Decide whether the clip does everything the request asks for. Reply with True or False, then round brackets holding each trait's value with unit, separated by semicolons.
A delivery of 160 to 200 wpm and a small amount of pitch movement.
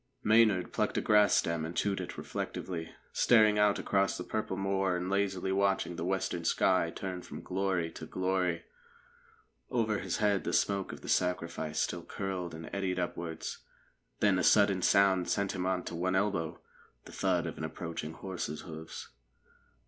True (170 wpm; 2.3 semitones)